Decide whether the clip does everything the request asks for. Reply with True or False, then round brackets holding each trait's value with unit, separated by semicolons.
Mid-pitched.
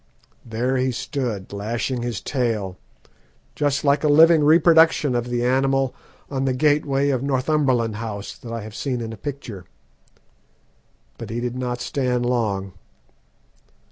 False (125 Hz)